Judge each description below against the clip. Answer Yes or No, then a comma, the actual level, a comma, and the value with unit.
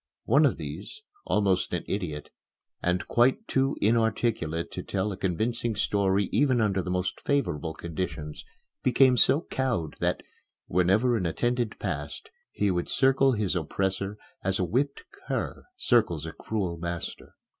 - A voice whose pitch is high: No, low, 100 Hz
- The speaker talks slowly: No, average, 145 wpm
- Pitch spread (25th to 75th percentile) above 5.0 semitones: Yes, wide, 5.5 semitones